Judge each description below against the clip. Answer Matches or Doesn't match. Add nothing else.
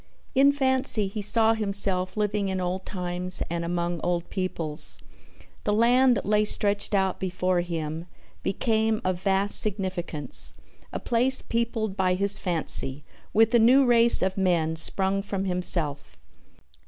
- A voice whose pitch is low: Doesn't match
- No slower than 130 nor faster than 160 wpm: Matches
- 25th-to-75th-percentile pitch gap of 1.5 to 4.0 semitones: Matches